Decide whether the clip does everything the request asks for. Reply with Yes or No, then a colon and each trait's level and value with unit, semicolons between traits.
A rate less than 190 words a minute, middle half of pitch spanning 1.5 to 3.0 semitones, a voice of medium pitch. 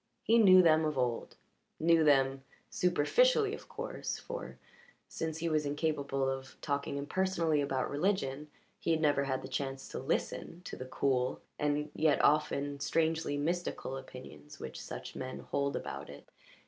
No: average, 155 wpm; average, 3.4 semitones; medium, 145 Hz